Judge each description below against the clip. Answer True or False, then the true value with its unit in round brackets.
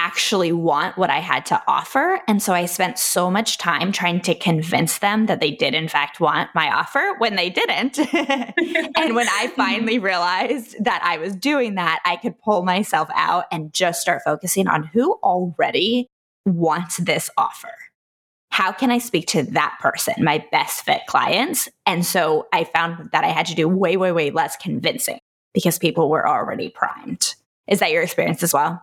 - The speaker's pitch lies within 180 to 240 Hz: True (185 Hz)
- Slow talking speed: False (185 wpm)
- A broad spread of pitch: True (5.8 semitones)